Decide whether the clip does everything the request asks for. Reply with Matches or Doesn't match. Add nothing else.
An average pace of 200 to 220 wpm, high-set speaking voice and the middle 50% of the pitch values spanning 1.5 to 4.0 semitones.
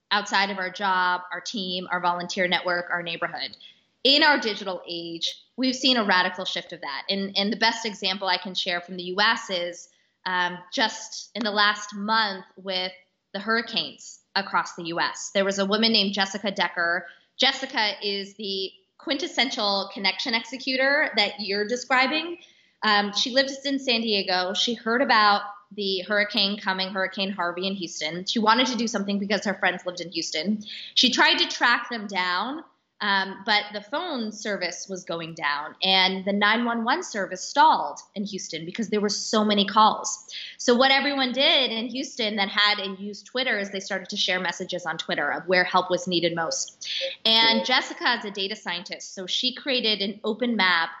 Doesn't match